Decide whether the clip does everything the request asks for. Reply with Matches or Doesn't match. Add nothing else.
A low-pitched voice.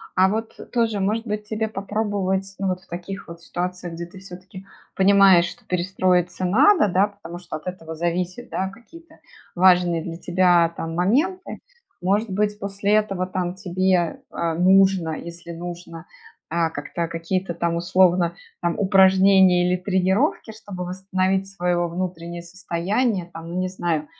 Doesn't match